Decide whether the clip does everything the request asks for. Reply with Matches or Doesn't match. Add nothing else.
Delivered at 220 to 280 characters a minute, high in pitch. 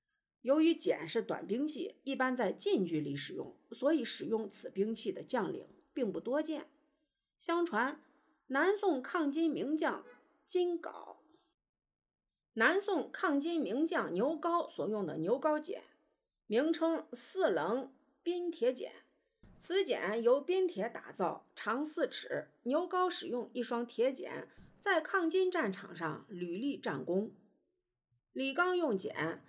Doesn't match